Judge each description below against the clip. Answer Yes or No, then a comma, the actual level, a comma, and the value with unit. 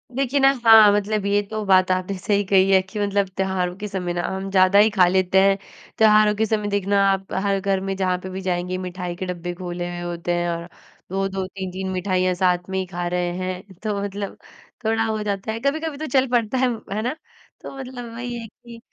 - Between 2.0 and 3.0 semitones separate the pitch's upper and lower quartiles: Yes, narrow, 2.6 semitones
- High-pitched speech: Yes, high, 195 Hz